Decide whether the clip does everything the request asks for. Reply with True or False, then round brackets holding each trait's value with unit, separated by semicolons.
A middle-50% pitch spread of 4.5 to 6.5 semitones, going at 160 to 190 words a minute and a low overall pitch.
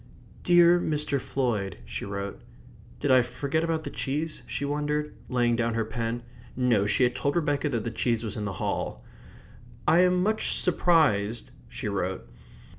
True (5.4 semitones; 165 wpm; 125 Hz)